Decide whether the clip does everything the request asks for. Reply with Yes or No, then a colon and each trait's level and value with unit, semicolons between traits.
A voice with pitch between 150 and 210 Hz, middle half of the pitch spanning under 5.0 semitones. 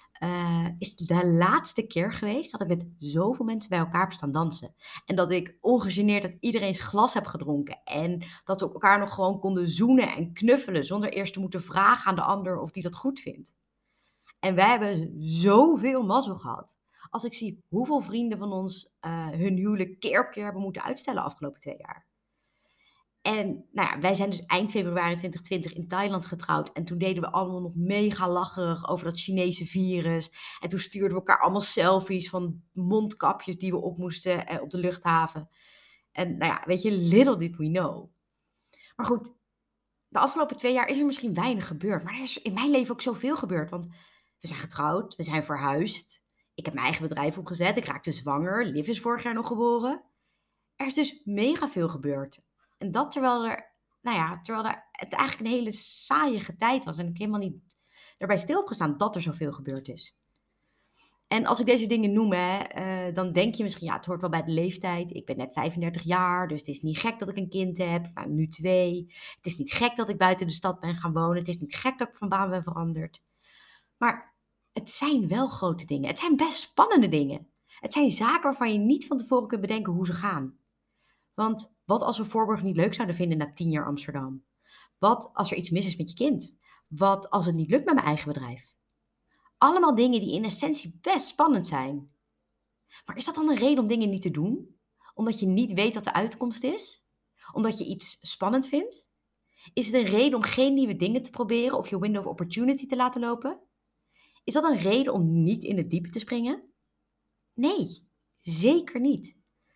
No: high, 190 Hz; wide, 5.6 semitones